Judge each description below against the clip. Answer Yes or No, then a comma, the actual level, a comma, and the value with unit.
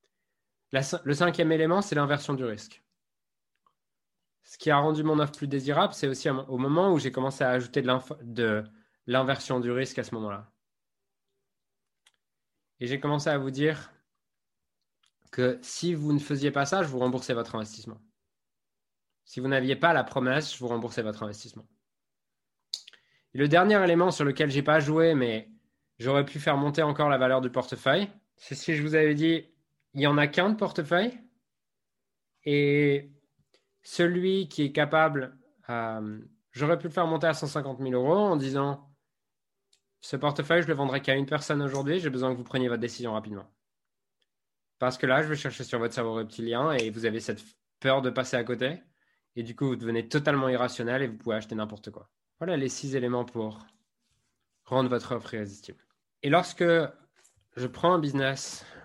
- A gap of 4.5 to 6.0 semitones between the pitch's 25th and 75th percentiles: No, average, 4.1 semitones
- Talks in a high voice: No, medium, 140 Hz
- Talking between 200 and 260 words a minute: No, average, 180 wpm